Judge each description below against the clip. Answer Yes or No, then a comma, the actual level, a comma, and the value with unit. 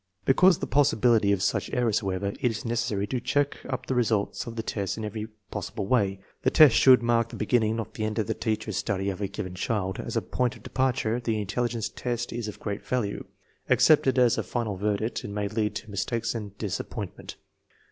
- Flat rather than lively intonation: No, average, 3.0 semitones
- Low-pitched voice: Yes, low, 110 Hz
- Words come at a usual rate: No, fast, 215 wpm